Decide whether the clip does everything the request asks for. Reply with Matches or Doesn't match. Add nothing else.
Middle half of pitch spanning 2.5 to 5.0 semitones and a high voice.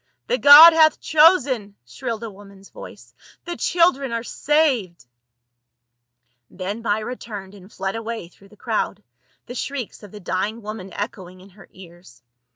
Doesn't match